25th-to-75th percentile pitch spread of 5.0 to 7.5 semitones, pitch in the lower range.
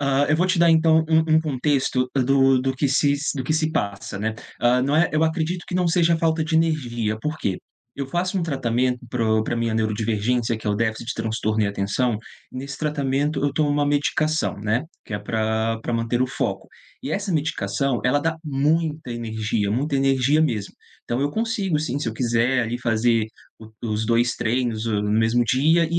Yes: wide, 5.4 semitones; low, 130 Hz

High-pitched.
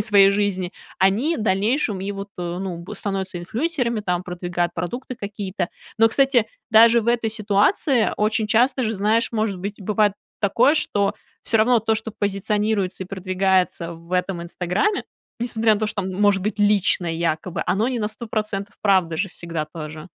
Yes: high, 205 Hz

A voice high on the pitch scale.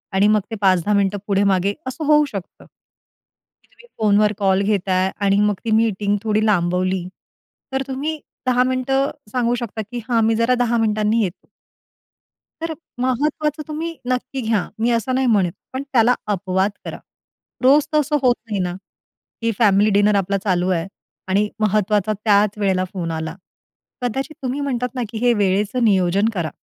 Yes: high, 215 Hz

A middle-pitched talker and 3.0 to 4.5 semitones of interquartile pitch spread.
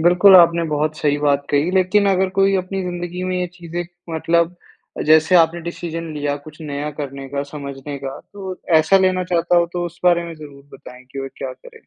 Yes: medium, 170 Hz; average, 3.6 semitones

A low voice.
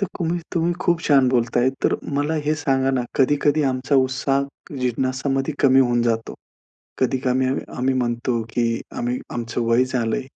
Yes: low, 130 Hz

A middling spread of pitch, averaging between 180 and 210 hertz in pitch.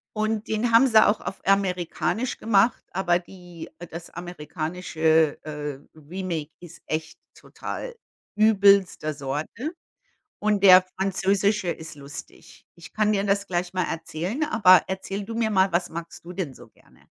Yes: average, 4.0 semitones; medium, 185 Hz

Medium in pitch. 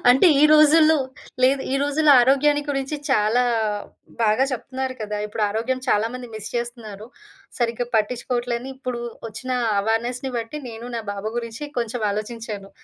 No: high, 240 Hz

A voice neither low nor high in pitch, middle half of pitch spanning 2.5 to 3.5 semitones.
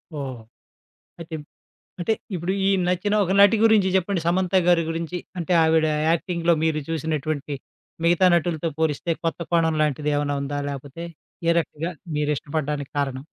Yes: medium, 160 Hz; average, 2.8 semitones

